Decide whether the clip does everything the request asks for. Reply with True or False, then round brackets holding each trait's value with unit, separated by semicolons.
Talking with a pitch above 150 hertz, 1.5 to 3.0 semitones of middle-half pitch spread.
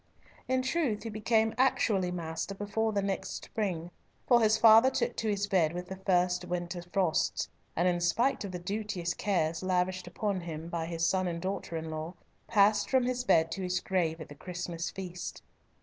False (185 Hz; 3.6 semitones)